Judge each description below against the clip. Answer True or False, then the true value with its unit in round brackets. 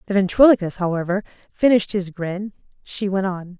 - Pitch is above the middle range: True (195 Hz)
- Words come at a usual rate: True (150 wpm)